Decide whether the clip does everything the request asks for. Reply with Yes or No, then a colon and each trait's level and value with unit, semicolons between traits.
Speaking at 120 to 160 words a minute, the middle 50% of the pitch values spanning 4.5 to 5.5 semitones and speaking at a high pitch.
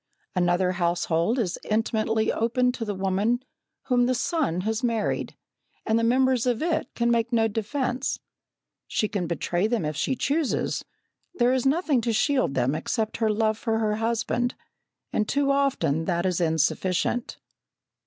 Yes: average, 155 wpm; average, 4.8 semitones; high, 225 Hz